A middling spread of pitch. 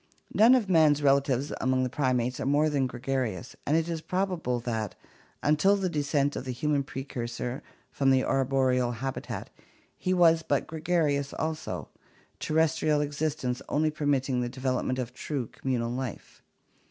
Yes: average, 3.4 semitones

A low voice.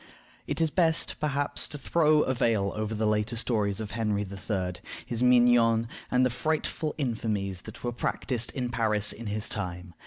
Yes: low, 115 Hz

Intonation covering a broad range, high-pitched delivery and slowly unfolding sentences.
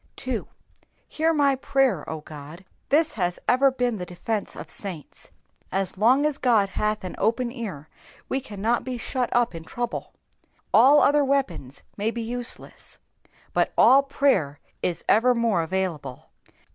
No: wide, 6.3 semitones; high, 230 Hz; average, 145 wpm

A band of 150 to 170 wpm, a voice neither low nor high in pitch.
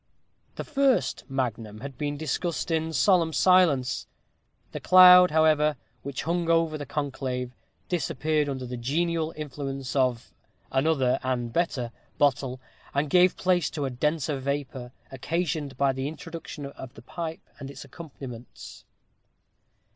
No: slow, 135 wpm; medium, 145 Hz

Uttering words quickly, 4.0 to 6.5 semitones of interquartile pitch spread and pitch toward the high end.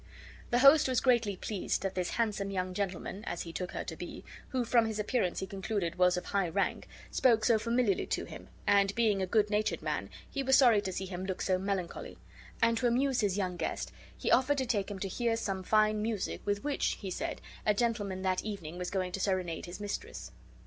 No: fast, 220 wpm; average, 3.6 semitones; high, 205 Hz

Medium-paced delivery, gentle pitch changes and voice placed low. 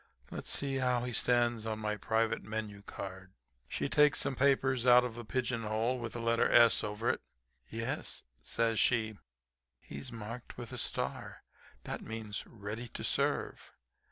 Yes: average, 160 wpm; narrow, 2.2 semitones; low, 115 Hz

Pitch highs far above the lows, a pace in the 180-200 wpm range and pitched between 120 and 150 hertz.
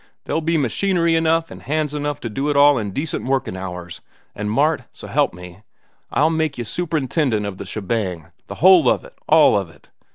Yes: wide, 7.3 semitones; average, 190 wpm; medium, 140 Hz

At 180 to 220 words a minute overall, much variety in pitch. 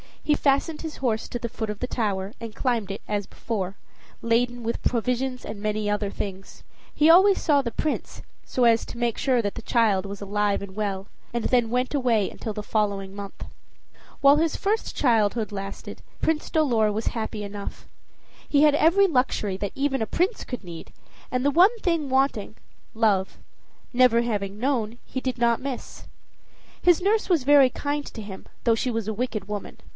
No: average, 185 wpm; average, 4.7 semitones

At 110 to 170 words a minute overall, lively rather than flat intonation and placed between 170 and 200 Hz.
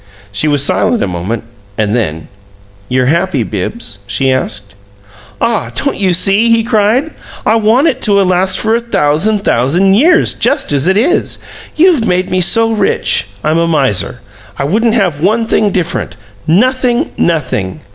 Yes: average, 160 wpm; wide, 8.1 semitones; high, 190 Hz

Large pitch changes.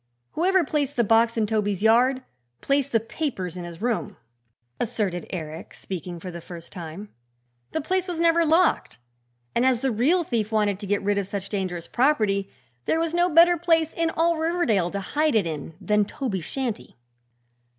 Yes: wide, 8.1 semitones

